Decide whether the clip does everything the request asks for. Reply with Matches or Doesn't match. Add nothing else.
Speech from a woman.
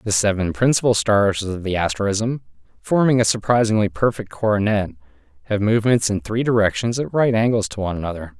Doesn't match